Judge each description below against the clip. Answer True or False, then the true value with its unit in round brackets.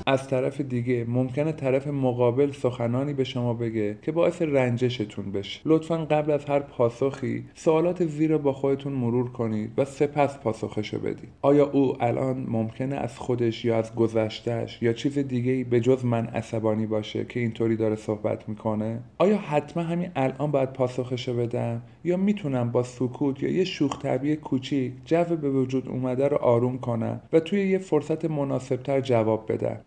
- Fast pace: True (165 wpm)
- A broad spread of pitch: False (3.5 semitones)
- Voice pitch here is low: True (130 Hz)